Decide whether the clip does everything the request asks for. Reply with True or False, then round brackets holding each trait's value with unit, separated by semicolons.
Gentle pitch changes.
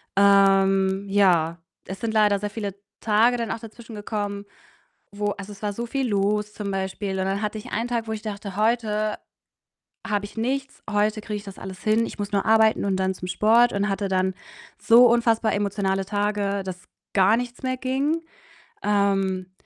True (2.3 semitones)